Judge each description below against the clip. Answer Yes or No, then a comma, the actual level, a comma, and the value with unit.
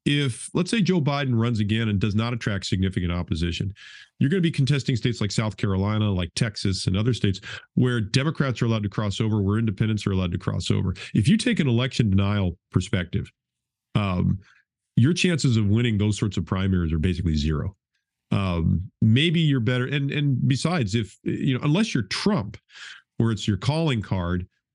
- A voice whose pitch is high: No, low, 110 Hz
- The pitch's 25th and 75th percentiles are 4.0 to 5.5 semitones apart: Yes, average, 5.2 semitones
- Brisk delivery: No, average, 190 wpm